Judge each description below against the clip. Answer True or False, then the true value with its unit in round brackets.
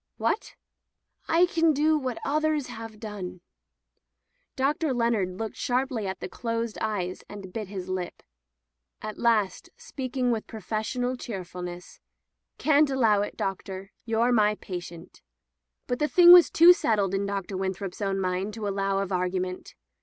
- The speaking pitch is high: True (215 Hz)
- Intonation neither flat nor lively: True (4.9 semitones)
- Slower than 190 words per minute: True (145 wpm)